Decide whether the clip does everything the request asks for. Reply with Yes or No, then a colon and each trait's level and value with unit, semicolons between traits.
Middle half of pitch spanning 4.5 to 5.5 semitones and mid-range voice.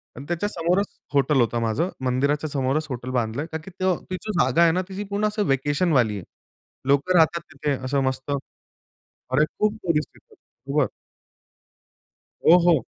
Yes: average, 5.1 semitones; medium, 150 Hz